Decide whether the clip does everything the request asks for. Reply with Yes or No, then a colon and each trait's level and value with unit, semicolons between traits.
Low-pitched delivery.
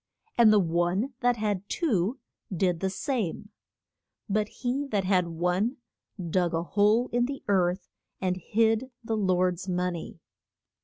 No: high, 195 Hz